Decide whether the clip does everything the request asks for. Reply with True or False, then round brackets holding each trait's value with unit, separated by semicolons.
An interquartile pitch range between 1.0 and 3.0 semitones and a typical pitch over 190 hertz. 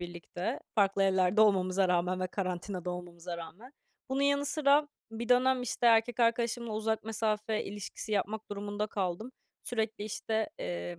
False (4.0 semitones; 210 Hz)